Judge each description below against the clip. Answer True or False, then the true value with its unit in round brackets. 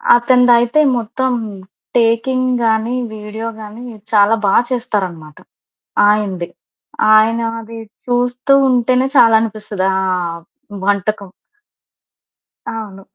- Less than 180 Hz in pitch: False (225 Hz)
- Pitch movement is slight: False (3.0 semitones)